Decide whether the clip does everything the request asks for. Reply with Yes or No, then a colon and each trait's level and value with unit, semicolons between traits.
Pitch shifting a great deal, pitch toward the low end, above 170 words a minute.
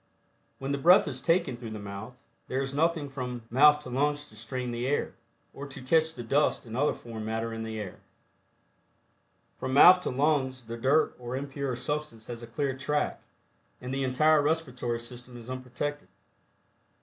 No: average, 3.5 semitones; low, 130 Hz; average, 180 wpm